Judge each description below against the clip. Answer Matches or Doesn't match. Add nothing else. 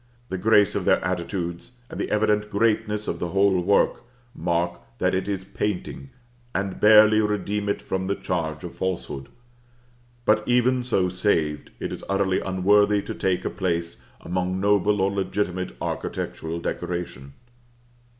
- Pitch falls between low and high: Doesn't match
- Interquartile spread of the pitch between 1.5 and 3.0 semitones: Matches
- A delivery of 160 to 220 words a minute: Doesn't match